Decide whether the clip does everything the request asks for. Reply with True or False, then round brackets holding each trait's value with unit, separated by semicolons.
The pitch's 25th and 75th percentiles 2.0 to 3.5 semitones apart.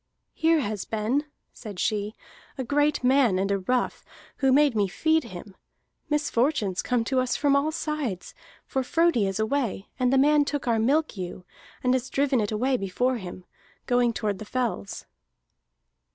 False (5.1 semitones)